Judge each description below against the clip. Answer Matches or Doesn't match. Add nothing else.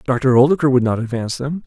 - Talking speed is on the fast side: Matches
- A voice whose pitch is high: Doesn't match